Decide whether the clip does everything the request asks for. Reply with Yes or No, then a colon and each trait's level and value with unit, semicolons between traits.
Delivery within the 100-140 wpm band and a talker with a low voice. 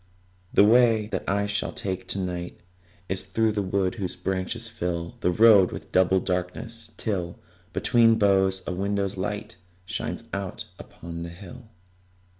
No: average, 155 wpm; very low, 95 Hz